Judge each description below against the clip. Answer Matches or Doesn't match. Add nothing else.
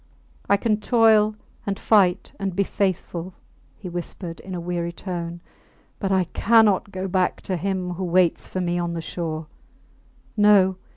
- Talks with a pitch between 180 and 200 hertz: Matches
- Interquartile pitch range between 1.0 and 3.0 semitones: Matches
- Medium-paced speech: Matches